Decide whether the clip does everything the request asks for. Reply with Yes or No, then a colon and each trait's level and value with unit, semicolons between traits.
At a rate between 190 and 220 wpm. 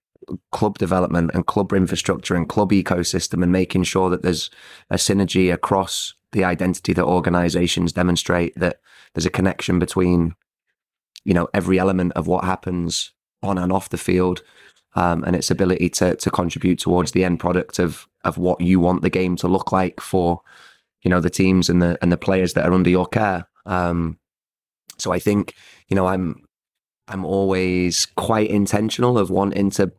No: average, 175 wpm